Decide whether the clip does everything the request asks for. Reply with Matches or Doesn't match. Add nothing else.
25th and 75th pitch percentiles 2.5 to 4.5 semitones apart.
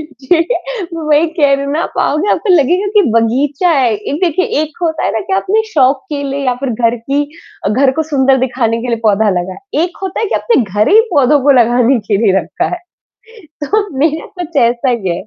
Doesn't match